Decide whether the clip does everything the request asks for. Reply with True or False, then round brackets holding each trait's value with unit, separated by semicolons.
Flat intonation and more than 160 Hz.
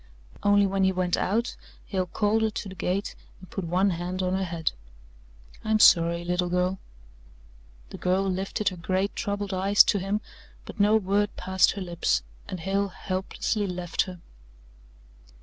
True (1.9 semitones; 190 Hz)